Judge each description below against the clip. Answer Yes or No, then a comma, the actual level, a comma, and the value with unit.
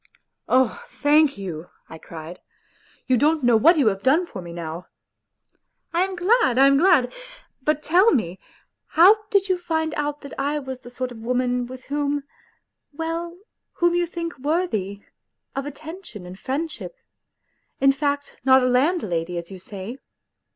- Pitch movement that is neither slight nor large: No, wide, 6.3 semitones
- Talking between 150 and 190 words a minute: Yes, average, 170 wpm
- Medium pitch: No, very high, 275 Hz